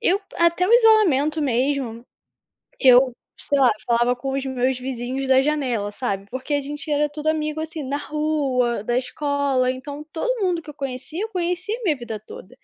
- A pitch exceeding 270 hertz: Yes, very high, 280 Hz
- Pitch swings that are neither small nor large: Yes, average, 3.6 semitones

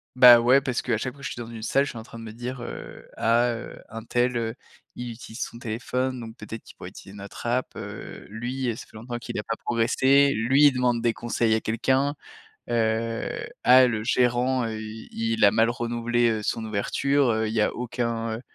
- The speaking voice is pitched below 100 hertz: No, low, 115 Hz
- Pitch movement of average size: No, narrow, 1.9 semitones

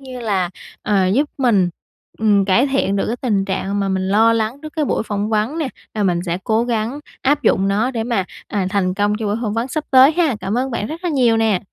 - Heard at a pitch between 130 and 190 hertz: No, high, 220 Hz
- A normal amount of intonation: Yes, average, 4.4 semitones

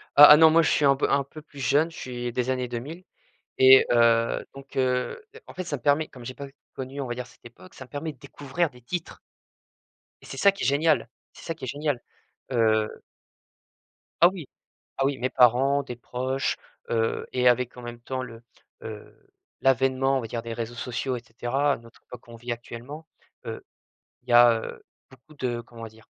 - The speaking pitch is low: Yes, low, 130 Hz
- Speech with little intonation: No, average, 3.0 semitones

